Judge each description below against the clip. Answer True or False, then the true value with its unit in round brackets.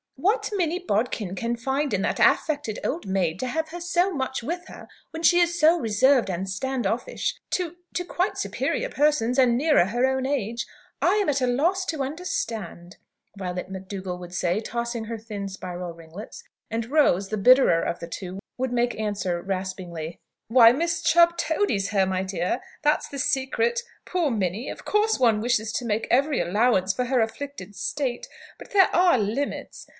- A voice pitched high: True (240 Hz)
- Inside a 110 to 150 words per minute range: False (180 wpm)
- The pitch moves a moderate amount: False (7.8 semitones)